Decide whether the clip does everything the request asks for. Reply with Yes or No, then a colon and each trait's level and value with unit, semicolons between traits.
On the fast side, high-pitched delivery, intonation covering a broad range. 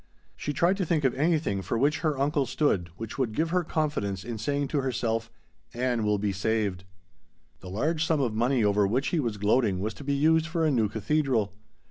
No: fast, 210 wpm; low, 130 Hz; wide, 6.0 semitones